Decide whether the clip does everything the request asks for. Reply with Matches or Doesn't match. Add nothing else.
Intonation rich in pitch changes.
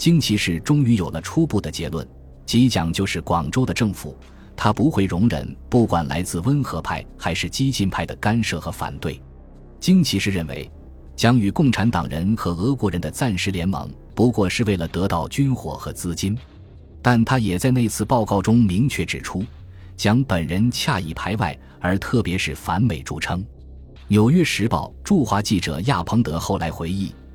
Matches